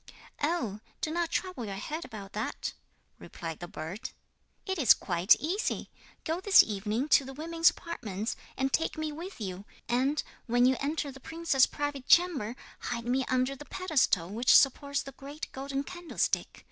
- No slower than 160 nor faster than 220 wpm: Yes, average, 165 wpm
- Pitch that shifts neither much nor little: No, wide, 6.1 semitones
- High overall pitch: Yes, very high, 270 Hz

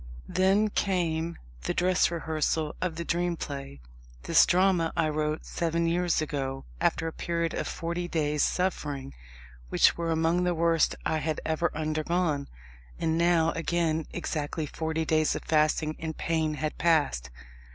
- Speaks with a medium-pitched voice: Yes, medium, 160 Hz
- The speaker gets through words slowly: No, average, 150 wpm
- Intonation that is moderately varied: No, narrow, 1.8 semitones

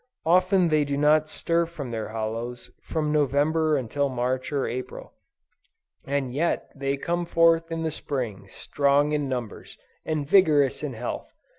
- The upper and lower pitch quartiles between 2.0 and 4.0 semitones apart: Yes, average, 3.7 semitones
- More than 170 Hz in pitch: No, medium, 145 Hz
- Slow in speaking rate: No, average, 150 wpm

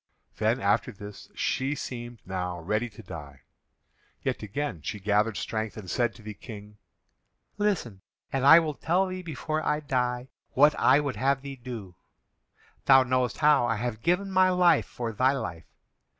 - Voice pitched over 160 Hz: No, low, 125 Hz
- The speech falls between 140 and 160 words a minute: No, average, 170 wpm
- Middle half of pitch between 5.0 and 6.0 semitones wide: Yes, wide, 5.6 semitones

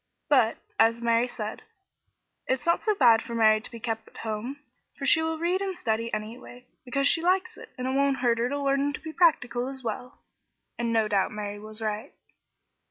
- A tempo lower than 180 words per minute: No, fast, 205 wpm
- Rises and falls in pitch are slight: No, average, 4.0 semitones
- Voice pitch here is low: No, high, 245 Hz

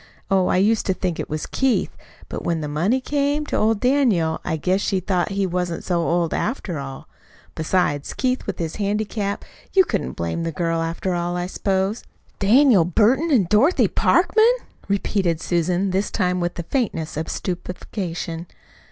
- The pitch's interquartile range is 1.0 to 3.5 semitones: No, average, 4.4 semitones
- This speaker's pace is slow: No, average, 170 wpm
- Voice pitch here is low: No, medium, 185 Hz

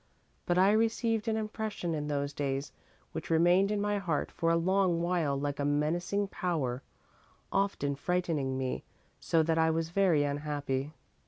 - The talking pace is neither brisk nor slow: Yes, average, 160 wpm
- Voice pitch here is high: No, medium, 165 Hz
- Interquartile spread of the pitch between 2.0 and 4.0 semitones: No, average, 5.1 semitones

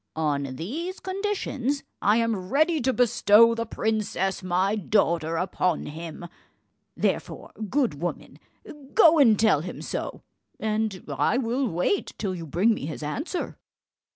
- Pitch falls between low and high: No, high, 215 Hz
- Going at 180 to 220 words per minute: No, slow, 135 wpm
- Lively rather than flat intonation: Yes, wide, 6.8 semitones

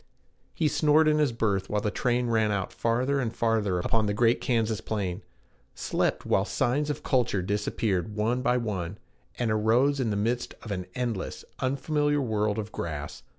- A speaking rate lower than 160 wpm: No, average, 175 wpm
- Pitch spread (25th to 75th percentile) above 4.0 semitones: No, average, 3.4 semitones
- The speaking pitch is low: Yes, low, 115 Hz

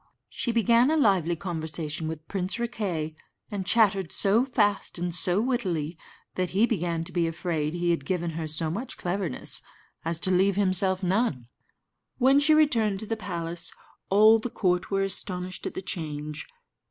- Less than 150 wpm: No, average, 165 wpm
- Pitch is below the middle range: No, medium, 185 Hz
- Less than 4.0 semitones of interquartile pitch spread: No, average, 4.4 semitones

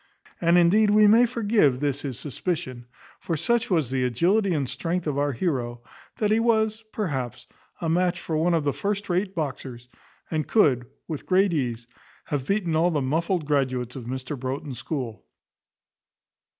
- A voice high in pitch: No, medium, 155 Hz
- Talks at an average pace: Yes, average, 165 wpm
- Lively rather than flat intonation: Yes, wide, 6.4 semitones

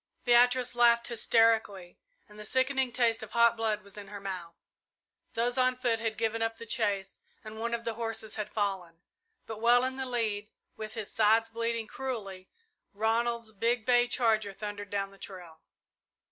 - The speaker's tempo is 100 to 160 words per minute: No, average, 175 wpm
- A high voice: Yes, high, 225 Hz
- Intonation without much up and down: Yes, narrow, 2.3 semitones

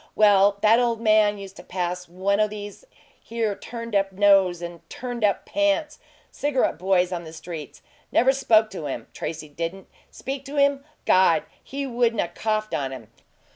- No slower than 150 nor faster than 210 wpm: Yes, average, 175 wpm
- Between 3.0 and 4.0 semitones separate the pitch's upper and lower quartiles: No, average, 4.7 semitones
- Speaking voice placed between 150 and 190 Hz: No, high, 205 Hz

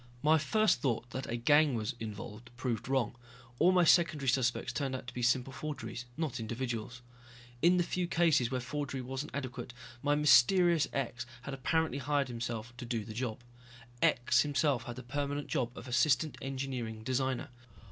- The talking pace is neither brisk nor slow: Yes, average, 170 wpm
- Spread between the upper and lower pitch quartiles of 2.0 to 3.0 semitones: No, average, 3.5 semitones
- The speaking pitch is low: Yes, low, 130 Hz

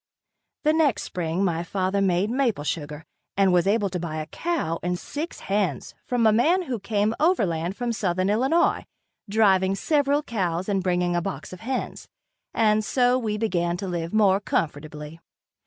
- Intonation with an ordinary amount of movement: Yes, average, 5.0 semitones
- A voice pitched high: Yes, high, 195 Hz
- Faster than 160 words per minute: Yes, average, 170 wpm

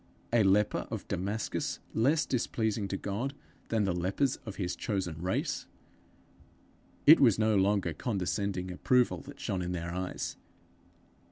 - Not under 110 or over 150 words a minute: Yes, average, 140 wpm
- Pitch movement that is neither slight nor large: Yes, average, 3.7 semitones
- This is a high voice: No, low, 100 Hz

